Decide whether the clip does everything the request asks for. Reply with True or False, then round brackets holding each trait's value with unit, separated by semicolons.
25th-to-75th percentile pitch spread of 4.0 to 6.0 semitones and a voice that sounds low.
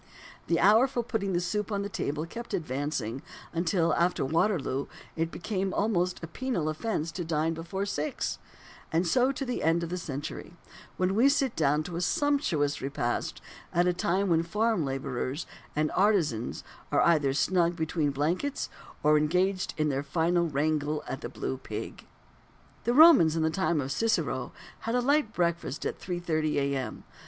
False (4.8 semitones; 170 Hz)